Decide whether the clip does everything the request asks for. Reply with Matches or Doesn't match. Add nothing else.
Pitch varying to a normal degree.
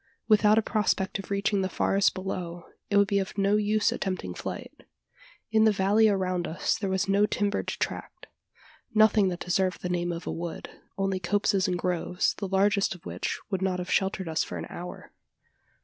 Doesn't match